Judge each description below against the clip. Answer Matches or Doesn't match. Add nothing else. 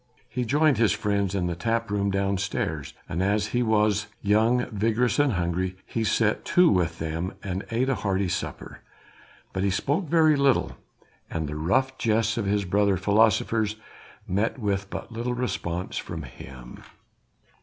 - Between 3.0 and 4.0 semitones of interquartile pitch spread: Matches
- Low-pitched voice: Matches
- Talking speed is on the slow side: Doesn't match